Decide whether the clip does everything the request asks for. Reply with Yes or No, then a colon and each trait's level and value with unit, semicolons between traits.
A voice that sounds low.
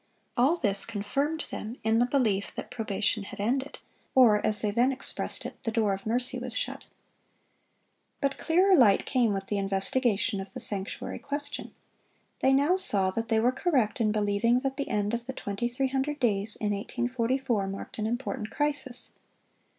No: high, 235 Hz